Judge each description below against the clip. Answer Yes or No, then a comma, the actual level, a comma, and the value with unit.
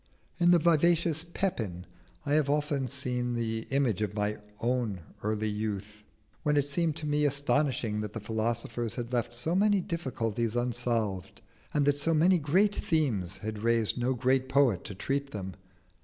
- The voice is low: Yes, low, 125 Hz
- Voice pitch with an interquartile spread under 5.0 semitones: No, average, 5.3 semitones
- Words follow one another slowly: No, average, 160 wpm